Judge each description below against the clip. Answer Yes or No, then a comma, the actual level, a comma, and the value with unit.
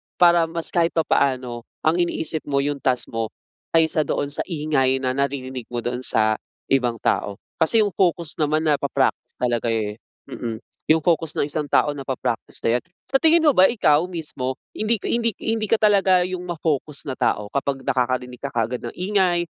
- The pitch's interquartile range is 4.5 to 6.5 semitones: Yes, average, 5.3 semitones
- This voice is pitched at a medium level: Yes, medium, 145 Hz